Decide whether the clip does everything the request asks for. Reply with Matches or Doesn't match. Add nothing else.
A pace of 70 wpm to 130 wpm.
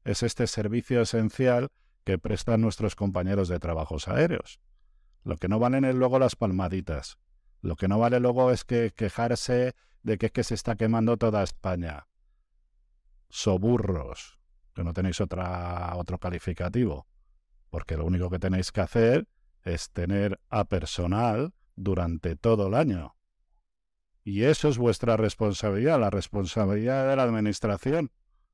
Doesn't match